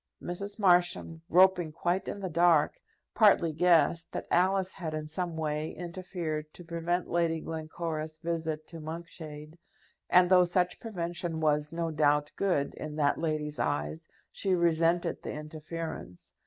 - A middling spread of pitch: No, narrow, 2.2 semitones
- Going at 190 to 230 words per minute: No, average, 140 wpm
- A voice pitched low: No, medium, 165 Hz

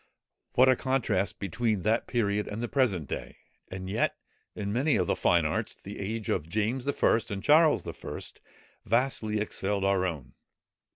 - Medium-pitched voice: No, low, 105 Hz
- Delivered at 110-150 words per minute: No, average, 165 wpm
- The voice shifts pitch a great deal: No, average, 3.8 semitones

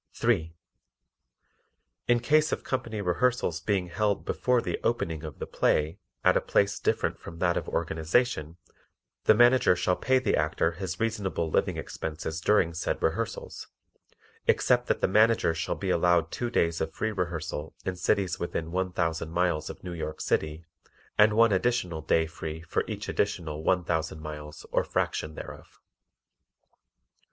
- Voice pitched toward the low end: Yes, very low, 85 Hz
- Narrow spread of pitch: No, average, 4.9 semitones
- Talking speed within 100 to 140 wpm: No, average, 155 wpm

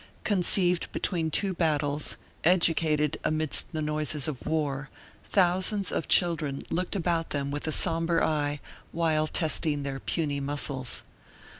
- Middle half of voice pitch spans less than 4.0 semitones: Yes, average, 2.7 semitones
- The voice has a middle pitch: Yes, medium, 155 Hz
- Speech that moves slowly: Yes, slow, 130 wpm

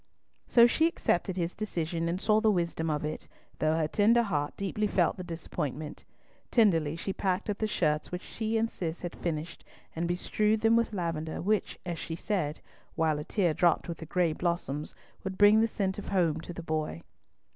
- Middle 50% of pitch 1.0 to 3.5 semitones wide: No, average, 4.3 semitones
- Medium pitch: Yes, medium, 175 Hz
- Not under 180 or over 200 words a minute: Yes, average, 195 wpm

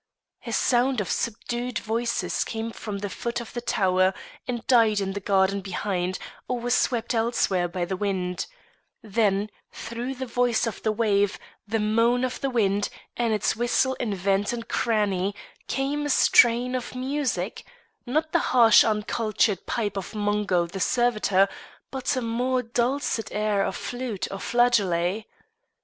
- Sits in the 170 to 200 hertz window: No, high, 225 Hz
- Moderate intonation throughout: Yes, average, 3.5 semitones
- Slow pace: No, average, 155 wpm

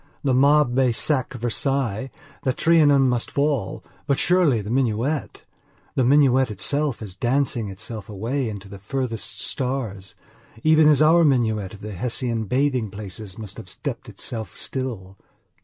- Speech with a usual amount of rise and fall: Yes, average, 4.5 semitones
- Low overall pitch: Yes, low, 125 Hz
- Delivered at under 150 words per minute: Yes, average, 140 wpm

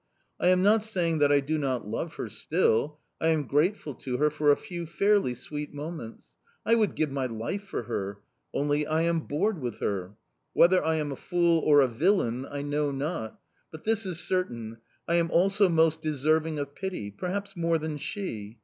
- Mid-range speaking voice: Yes, medium, 155 Hz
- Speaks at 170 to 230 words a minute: Yes, average, 195 wpm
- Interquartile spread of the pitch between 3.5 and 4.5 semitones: Yes, average, 4.2 semitones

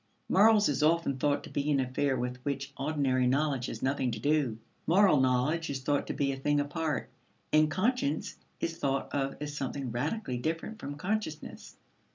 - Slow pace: No, average, 180 wpm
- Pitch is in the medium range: Yes, medium, 145 Hz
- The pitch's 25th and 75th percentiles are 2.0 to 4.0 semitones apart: Yes, average, 2.9 semitones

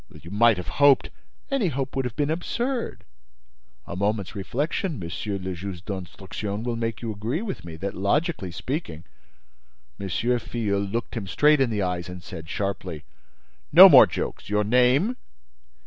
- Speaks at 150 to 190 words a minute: Yes, average, 160 wpm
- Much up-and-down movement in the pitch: Yes, wide, 6.2 semitones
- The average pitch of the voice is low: Yes, low, 105 Hz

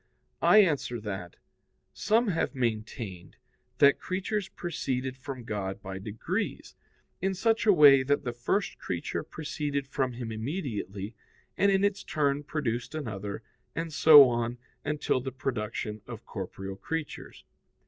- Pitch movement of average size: No, wide, 6.0 semitones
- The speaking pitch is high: No, low, 130 Hz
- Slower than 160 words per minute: Yes, slow, 135 wpm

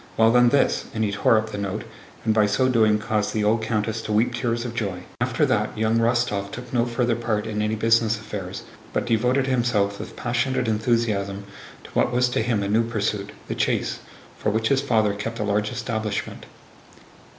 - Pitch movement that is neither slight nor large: No, narrow, 2.1 semitones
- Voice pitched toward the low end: Yes, low, 110 Hz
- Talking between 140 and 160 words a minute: No, average, 195 wpm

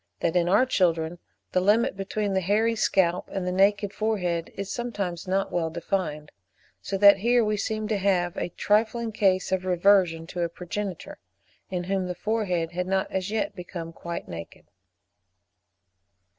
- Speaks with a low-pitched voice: No, high, 190 Hz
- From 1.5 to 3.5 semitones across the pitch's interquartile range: Yes, average, 2.9 semitones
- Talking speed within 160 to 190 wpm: Yes, average, 170 wpm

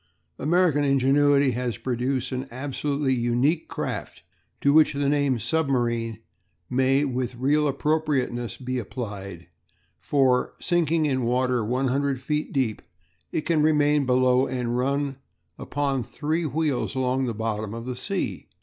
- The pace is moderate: No, slow, 130 wpm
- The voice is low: Yes, low, 130 Hz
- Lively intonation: No, average, 2.8 semitones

